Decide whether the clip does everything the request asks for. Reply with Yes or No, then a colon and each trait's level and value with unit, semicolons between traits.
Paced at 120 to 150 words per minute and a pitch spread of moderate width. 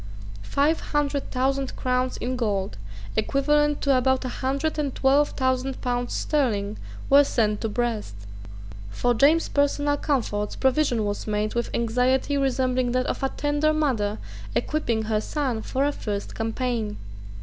Yes: average, 145 wpm; average, 4.0 semitones